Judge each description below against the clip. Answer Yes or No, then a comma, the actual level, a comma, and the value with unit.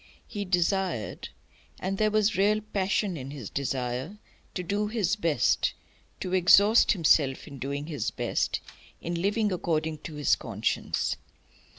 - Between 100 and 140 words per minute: Yes, slow, 135 wpm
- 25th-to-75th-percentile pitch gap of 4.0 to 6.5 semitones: Yes, wide, 5.6 semitones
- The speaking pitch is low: No, medium, 180 Hz